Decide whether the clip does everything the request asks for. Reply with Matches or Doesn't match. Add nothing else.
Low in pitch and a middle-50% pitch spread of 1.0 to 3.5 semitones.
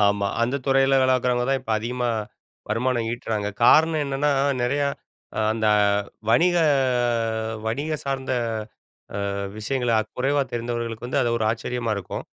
Matches